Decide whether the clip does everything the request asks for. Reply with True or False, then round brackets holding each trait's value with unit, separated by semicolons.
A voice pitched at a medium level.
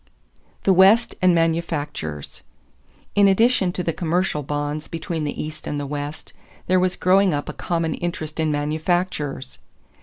True (165 Hz)